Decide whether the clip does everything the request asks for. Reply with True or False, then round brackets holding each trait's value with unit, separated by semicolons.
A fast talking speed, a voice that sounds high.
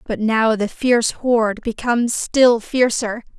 False (140 wpm; 230 Hz)